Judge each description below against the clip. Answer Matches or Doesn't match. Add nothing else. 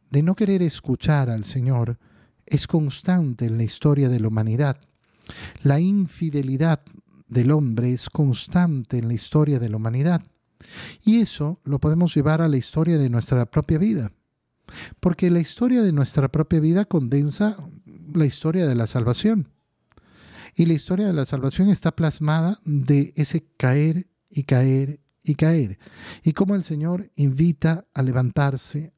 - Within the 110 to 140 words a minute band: Doesn't match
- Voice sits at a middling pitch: Matches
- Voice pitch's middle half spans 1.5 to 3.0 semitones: Doesn't match